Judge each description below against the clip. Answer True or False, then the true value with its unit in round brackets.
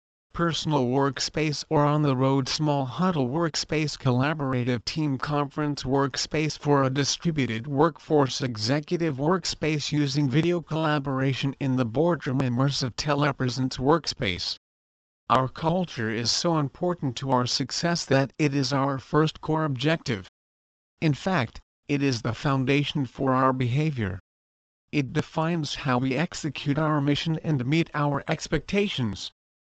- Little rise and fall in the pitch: False (3.2 semitones)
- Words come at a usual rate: False (130 wpm)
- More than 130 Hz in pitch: True (140 Hz)